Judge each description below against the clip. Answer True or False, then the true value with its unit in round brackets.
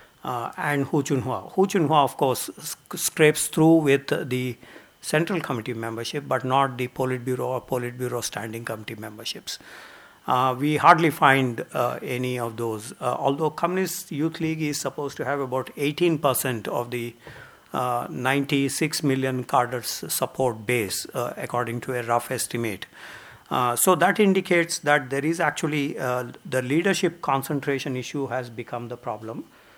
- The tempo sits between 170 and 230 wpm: False (155 wpm)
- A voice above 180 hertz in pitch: False (135 Hz)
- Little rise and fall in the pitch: False (3.8 semitones)